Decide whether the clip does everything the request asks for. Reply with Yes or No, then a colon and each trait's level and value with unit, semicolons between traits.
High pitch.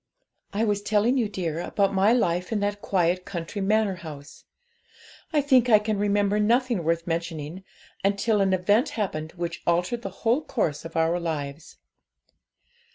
Yes: high, 195 Hz